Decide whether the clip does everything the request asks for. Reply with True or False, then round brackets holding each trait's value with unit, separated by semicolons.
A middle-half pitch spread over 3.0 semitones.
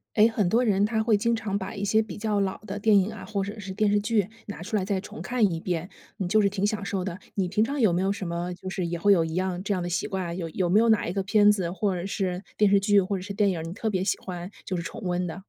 False (2.6 semitones)